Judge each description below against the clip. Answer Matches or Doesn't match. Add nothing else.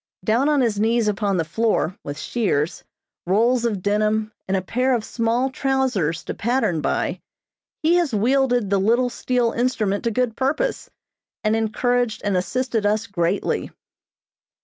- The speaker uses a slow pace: Doesn't match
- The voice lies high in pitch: Matches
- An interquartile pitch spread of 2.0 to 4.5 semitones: Matches